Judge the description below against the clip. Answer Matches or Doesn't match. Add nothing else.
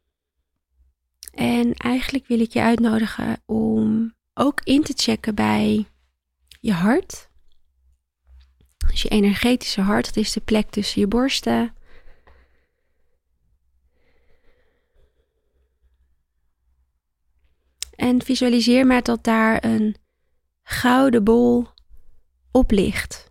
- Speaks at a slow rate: Matches